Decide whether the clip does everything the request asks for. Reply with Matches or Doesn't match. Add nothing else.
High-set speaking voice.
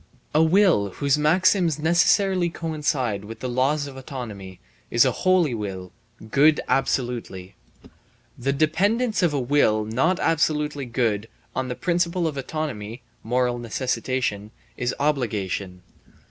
Doesn't match